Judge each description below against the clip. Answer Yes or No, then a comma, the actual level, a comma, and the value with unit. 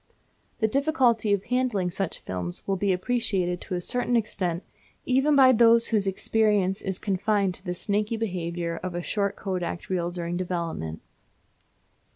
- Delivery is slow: No, average, 155 wpm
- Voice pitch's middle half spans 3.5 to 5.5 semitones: Yes, average, 4.1 semitones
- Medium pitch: No, high, 195 Hz